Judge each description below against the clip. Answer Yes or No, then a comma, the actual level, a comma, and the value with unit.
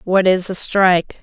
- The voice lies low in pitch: No, medium, 185 Hz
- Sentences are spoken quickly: No, average, 195 wpm